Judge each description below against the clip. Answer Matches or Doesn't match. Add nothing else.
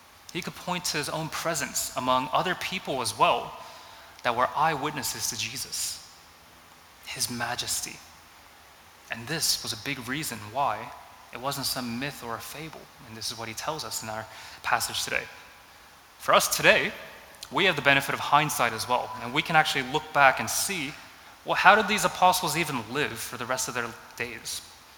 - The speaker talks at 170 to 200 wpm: Matches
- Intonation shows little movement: Doesn't match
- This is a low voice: Matches